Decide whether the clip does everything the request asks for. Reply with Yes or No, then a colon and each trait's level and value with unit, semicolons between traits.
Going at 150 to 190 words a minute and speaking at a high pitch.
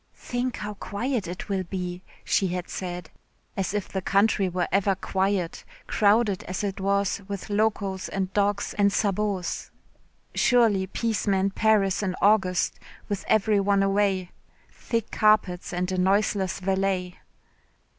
No: average, 140 wpm; high, 195 Hz